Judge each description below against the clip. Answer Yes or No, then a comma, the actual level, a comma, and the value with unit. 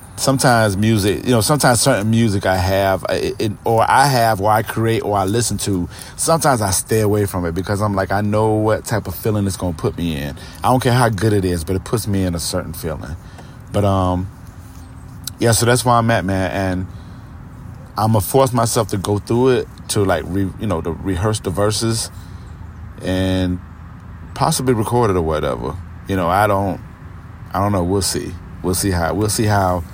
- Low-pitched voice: Yes, low, 100 Hz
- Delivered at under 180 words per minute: No, fast, 205 wpm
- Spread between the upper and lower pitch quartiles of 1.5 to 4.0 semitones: Yes, average, 3.6 semitones